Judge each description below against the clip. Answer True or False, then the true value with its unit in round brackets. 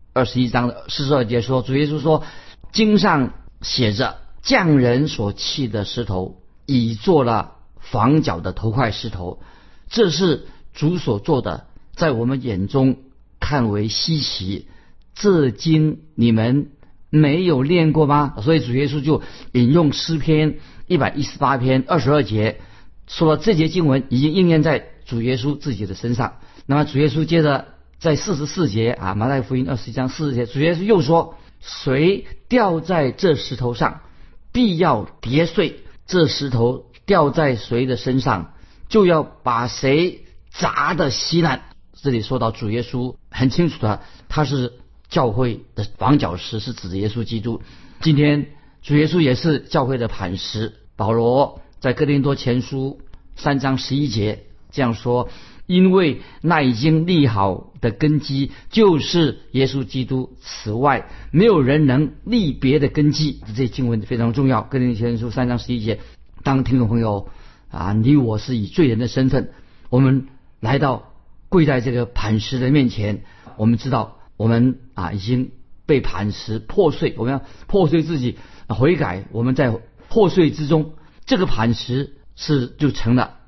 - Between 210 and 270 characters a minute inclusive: True (230 characters per minute)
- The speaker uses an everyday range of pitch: True (4.6 semitones)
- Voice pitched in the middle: False (130 Hz)